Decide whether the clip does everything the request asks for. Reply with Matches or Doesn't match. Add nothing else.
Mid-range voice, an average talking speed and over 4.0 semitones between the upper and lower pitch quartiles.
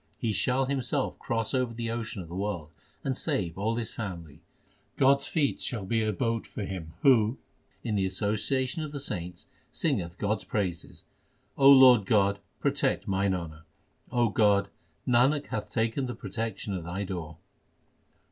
Doesn't match